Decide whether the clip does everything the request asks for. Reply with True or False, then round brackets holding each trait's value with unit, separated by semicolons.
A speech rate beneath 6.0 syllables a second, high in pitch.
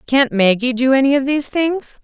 True (5.3 syllables/s; 265 Hz)